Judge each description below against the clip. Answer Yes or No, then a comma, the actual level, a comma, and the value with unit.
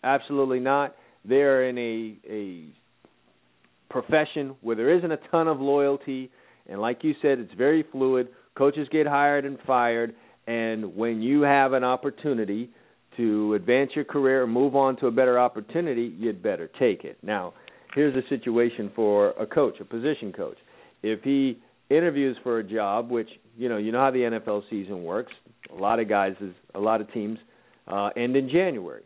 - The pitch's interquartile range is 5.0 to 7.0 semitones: No, average, 3.8 semitones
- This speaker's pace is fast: No, average, 180 wpm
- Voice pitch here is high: No, low, 125 Hz